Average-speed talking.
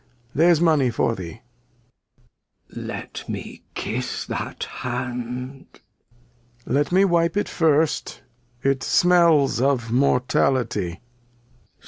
No: slow, 100 wpm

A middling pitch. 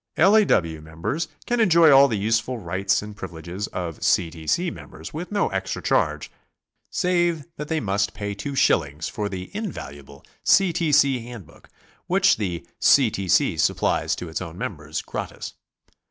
No: low, 105 Hz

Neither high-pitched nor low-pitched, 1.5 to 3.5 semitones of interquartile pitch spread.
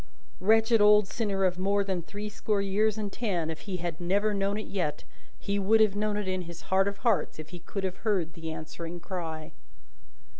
No: high, 195 Hz; average, 3.1 semitones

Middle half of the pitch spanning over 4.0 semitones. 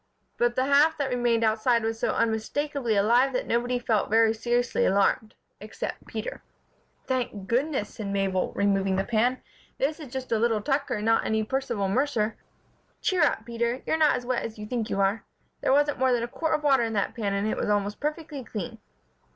No: average, 3.6 semitones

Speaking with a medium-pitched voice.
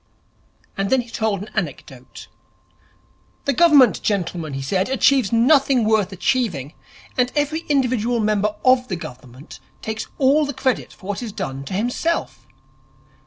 No: high, 220 Hz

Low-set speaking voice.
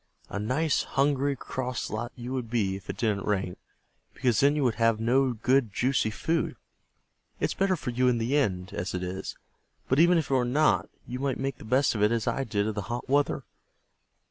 Yes: low, 125 Hz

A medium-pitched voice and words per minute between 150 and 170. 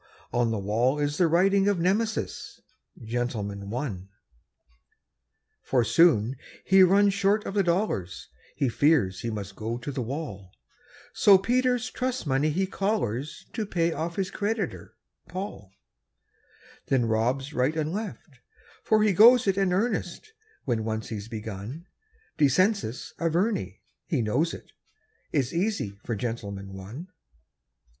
No: medium, 150 Hz; slow, 135 wpm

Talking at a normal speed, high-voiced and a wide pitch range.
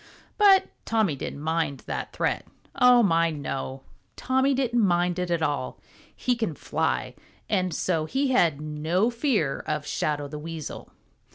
No: average, 150 wpm; medium, 170 Hz; wide, 7.8 semitones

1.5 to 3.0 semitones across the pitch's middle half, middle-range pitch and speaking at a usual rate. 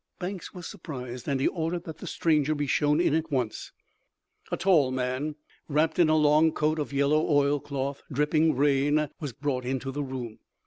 Yes: average, 2.7 semitones; medium, 145 Hz; average, 180 wpm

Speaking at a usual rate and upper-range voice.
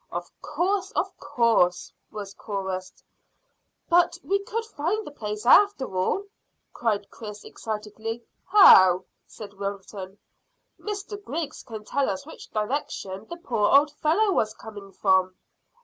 No: slow, 130 wpm; high, 225 Hz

